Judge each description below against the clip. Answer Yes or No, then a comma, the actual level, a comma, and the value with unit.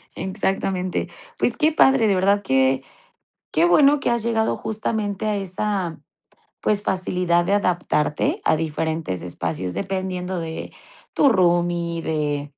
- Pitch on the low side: No, medium, 185 Hz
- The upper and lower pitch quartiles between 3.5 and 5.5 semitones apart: Yes, average, 4.0 semitones